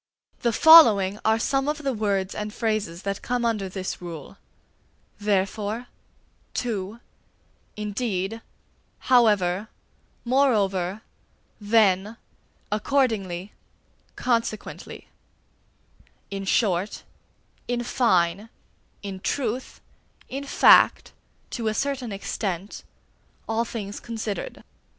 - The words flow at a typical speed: No, slow, 90 wpm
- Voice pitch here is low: No, high, 215 Hz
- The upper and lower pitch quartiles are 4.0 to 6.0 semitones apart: No, average, 3.3 semitones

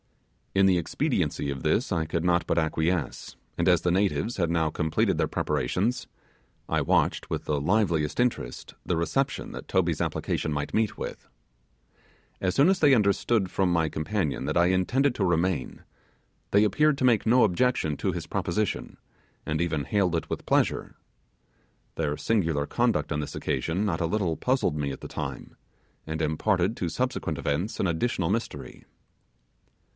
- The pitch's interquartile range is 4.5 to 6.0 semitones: Yes, average, 5.1 semitones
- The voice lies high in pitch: No, very low, 90 Hz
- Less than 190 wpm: Yes, average, 165 wpm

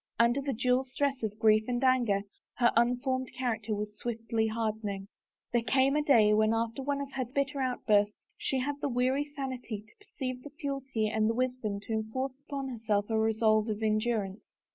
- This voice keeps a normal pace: Yes, average, 185 wpm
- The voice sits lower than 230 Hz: No, high, 240 Hz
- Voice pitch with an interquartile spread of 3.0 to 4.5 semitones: Yes, average, 3.5 semitones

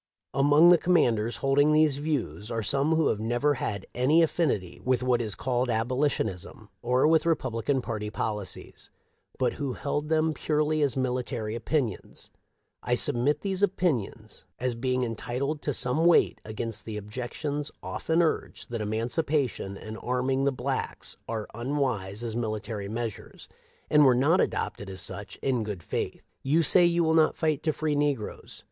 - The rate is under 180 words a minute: Yes, average, 165 wpm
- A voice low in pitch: Yes, low, 130 Hz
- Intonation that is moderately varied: Yes, average, 5.0 semitones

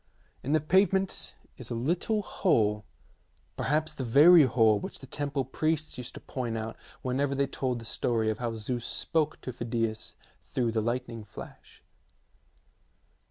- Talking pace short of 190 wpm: Yes, average, 160 wpm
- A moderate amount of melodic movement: Yes, average, 4.8 semitones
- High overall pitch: No, low, 125 Hz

